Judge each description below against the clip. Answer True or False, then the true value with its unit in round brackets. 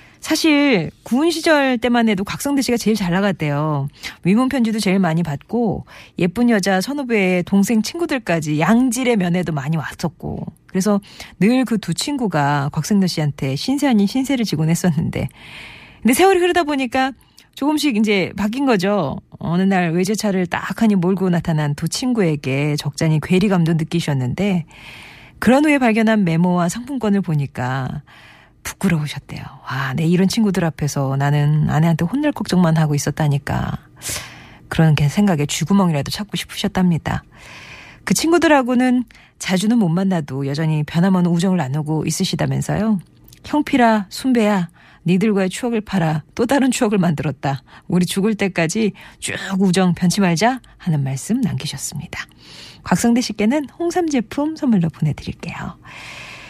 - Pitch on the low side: False (190 Hz)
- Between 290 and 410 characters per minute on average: True (330 characters per minute)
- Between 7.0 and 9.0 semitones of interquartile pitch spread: False (6.5 semitones)